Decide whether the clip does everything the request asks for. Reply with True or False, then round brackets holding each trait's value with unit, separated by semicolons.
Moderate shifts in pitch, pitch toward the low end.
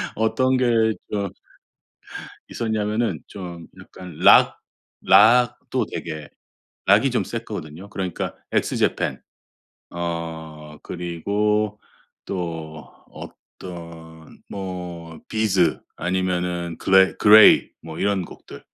True (3.9 semitones; 90 Hz)